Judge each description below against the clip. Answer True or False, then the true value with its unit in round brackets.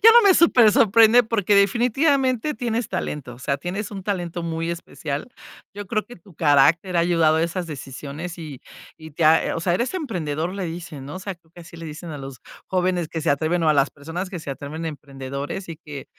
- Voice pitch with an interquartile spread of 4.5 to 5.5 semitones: True (4.8 semitones)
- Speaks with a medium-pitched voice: True (170 Hz)